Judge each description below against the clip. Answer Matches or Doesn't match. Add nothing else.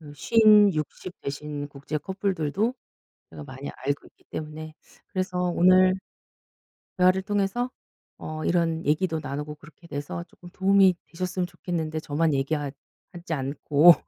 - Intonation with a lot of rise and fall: Doesn't match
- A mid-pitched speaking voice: Matches